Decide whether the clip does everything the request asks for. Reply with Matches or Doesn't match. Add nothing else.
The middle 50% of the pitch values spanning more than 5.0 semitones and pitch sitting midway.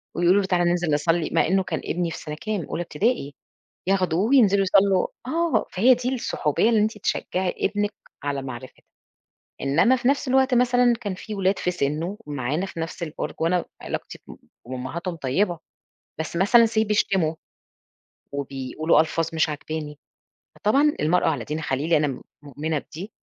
Matches